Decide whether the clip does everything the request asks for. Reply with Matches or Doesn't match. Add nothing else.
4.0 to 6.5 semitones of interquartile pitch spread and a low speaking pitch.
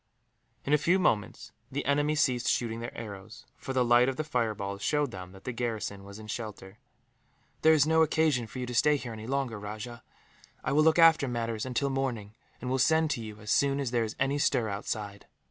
Matches